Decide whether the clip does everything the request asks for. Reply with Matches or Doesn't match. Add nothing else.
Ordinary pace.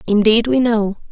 Matches